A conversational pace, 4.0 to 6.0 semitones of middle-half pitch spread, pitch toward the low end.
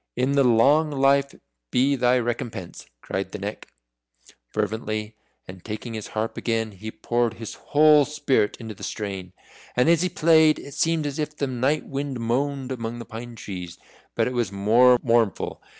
Yes: average, 165 wpm; average, 4.3 semitones; low, 120 Hz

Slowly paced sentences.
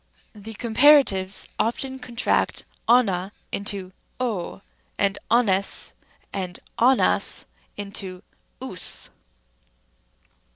Yes: slow, 80 wpm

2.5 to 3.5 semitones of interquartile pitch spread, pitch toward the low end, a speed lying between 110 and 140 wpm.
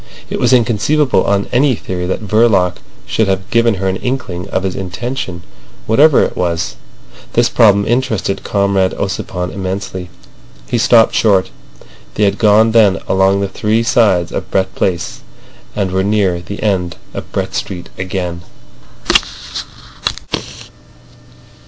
Yes: average, 3.2 semitones; low, 100 Hz; slow, 135 wpm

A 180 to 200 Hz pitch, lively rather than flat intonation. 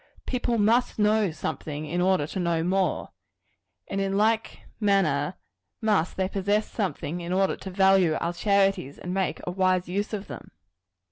No: high, 190 Hz; average, 2.7 semitones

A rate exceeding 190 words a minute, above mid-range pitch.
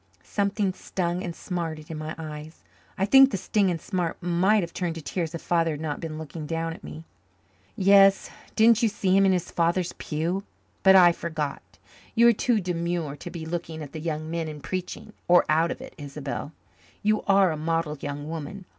No: average, 200 wpm; medium, 170 Hz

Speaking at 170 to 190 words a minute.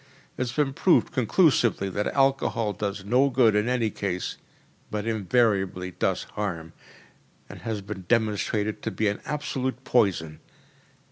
No: average, 145 wpm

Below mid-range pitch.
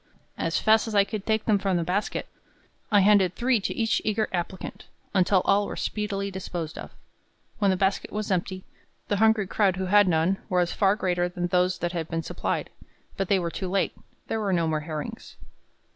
No: high, 190 Hz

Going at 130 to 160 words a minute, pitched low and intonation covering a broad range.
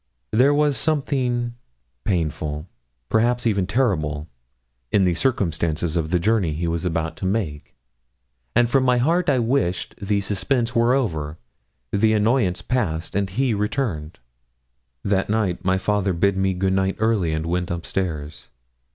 Yes: average, 145 wpm; low, 100 Hz; wide, 6.0 semitones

